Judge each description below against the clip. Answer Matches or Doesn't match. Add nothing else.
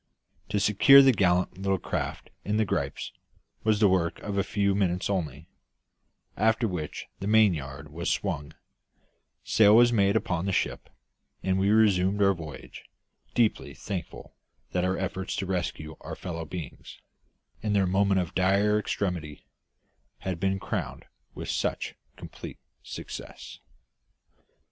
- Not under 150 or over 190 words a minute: Doesn't match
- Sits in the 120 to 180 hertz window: Doesn't match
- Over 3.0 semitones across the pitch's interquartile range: Doesn't match